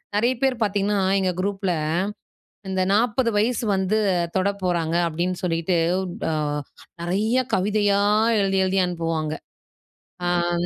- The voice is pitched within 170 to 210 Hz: Yes, high, 190 Hz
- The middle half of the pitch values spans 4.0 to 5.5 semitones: No, average, 3.0 semitones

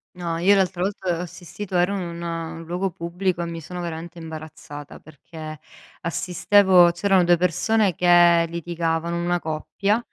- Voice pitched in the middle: Yes, medium, 175 Hz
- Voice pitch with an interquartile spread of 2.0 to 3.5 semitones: No, narrow, 1.6 semitones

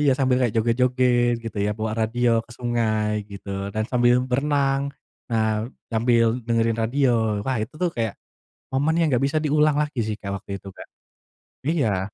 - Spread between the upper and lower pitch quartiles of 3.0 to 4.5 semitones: Yes, average, 3.5 semitones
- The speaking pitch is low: Yes, low, 120 Hz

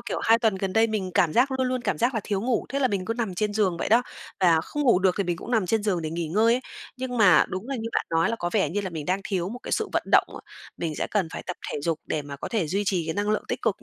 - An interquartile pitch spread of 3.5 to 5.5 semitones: Yes, average, 4.7 semitones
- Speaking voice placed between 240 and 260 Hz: No, high, 200 Hz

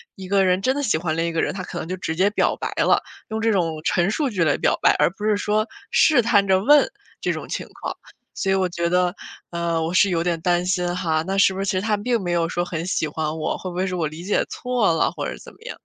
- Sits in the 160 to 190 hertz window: Yes, medium, 185 Hz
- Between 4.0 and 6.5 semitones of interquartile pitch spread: No, average, 3.2 semitones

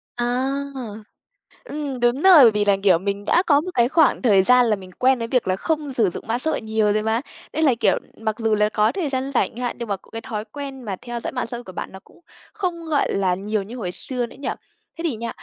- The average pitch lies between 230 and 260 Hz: Yes, high, 240 Hz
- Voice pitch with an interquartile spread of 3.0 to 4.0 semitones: No, average, 4.6 semitones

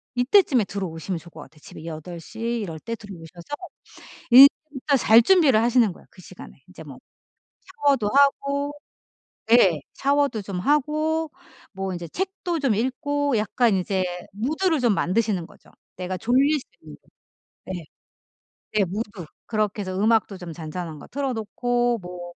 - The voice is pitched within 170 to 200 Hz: No, high, 220 Hz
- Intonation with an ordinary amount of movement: No, wide, 7.0 semitones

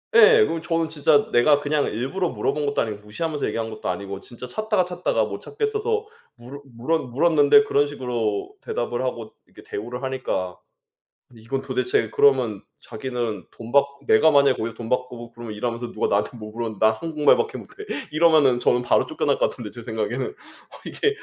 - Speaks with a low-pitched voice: Yes, low, 125 Hz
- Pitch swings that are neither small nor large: Yes, average, 4.9 semitones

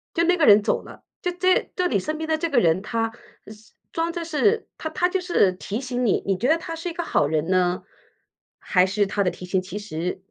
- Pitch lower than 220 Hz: No, high, 230 Hz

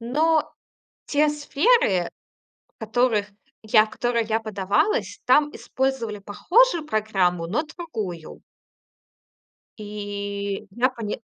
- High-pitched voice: Yes, high, 220 Hz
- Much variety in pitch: Yes, wide, 6.3 semitones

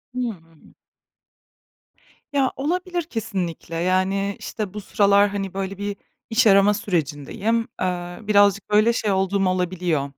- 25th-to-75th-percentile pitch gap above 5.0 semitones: No, narrow, 2.6 semitones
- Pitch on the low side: No, high, 200 Hz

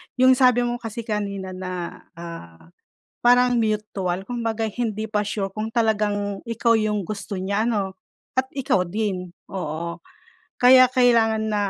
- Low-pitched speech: No, high, 215 Hz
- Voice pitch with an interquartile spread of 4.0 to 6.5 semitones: No, average, 3.5 semitones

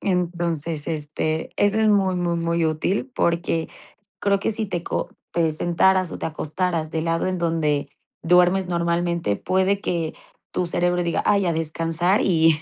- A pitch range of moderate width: No, narrow, 2.1 semitones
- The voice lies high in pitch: No, medium, 170 Hz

